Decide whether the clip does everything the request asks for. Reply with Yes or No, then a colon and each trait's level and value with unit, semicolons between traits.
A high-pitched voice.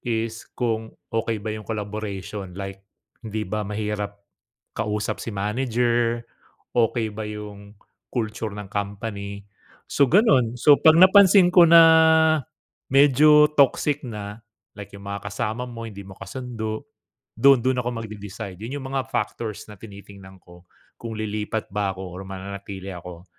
No: low, 110 Hz